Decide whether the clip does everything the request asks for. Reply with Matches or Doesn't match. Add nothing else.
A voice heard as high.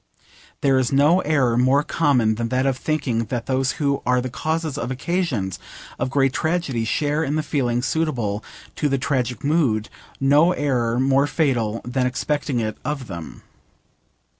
Doesn't match